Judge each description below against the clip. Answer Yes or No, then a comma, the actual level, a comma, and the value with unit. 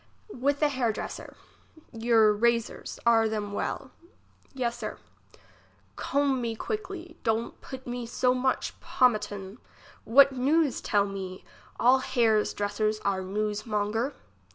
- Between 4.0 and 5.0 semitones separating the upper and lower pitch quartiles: No, average, 3.6 semitones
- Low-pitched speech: No, high, 235 Hz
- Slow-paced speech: Yes, slow, 125 wpm